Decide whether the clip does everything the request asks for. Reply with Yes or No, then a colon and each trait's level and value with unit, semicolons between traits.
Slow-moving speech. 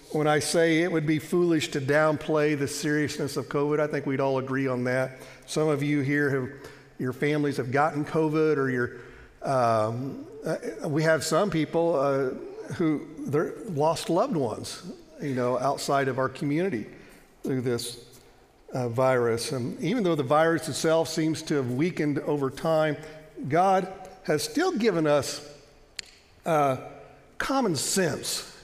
No: average, 150 wpm